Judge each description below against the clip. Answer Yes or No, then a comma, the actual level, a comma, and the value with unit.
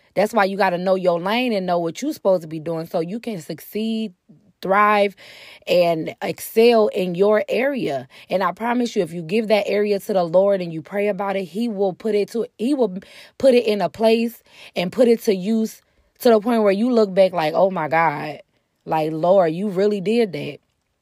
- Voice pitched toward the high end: Yes, high, 200 Hz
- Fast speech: Yes, fast, 220 wpm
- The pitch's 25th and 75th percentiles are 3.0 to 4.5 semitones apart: Yes, average, 3.6 semitones